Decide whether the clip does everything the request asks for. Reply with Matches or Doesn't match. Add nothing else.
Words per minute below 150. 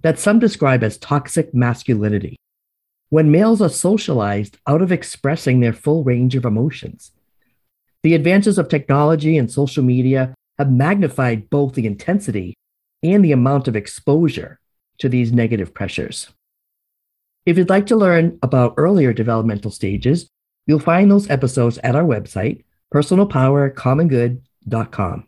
Matches